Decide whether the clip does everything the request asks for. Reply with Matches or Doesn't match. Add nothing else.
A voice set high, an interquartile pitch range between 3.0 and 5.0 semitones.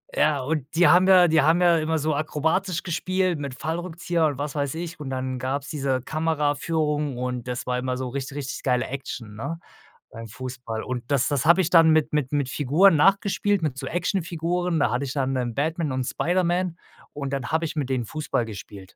Doesn't match